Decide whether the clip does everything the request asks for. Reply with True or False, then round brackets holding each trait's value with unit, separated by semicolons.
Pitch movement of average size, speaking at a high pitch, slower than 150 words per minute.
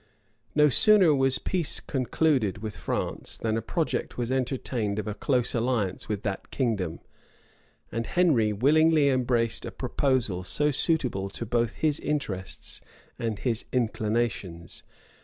False (4.8 semitones; 120 Hz; 140 wpm)